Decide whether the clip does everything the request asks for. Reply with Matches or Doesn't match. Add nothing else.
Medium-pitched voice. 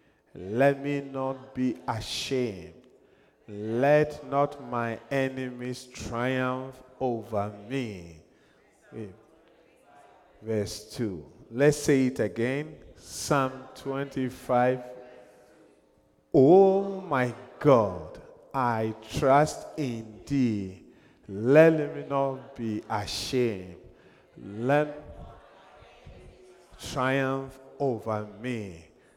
Doesn't match